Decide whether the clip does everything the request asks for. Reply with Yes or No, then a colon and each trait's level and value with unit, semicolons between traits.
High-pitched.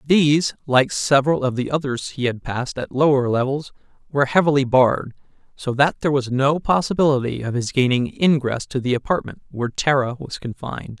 No: low, 135 Hz